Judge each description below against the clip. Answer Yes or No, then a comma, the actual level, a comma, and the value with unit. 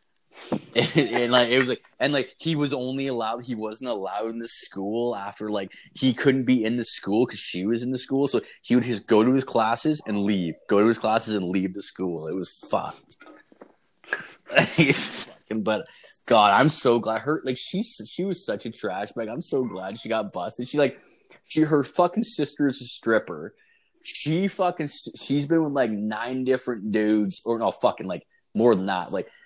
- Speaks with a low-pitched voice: Yes, low, 125 Hz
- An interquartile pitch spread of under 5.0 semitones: No, wide, 5.6 semitones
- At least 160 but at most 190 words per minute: No, fast, 205 wpm